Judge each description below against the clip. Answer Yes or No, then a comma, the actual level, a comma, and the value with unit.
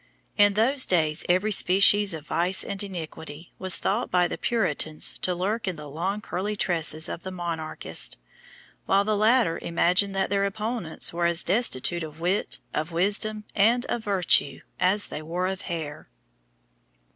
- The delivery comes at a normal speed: Yes, average, 160 wpm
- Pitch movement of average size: Yes, average, 3.5 semitones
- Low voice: No, medium, 185 Hz